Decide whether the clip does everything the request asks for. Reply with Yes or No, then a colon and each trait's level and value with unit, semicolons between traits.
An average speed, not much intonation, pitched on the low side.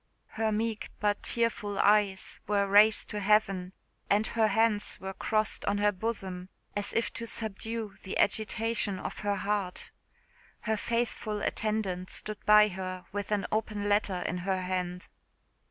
No: average, 150 wpm; narrow, 2.1 semitones; high, 205 Hz